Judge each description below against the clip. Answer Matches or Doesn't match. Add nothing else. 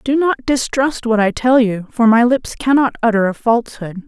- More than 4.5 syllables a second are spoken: Matches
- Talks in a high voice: Matches